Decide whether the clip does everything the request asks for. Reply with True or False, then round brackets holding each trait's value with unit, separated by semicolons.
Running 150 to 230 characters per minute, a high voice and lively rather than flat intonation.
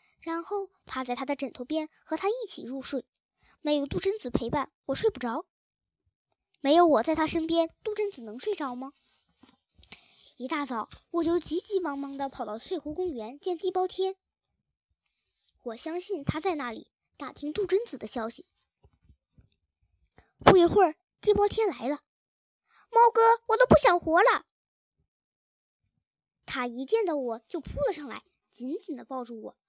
True (220 characters per minute; 320 Hz; 6.0 semitones)